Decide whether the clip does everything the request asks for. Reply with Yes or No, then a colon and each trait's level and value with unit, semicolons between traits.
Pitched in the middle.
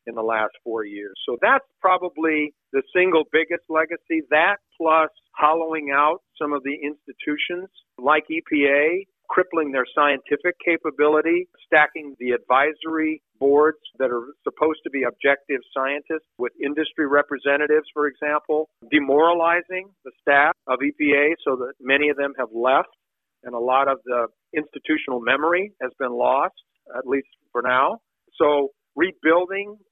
Yes: medium, 150 Hz